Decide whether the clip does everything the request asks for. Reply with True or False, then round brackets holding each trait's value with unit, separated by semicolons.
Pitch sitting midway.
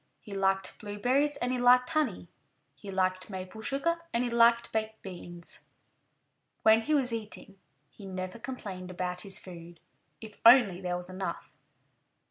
False (205 Hz)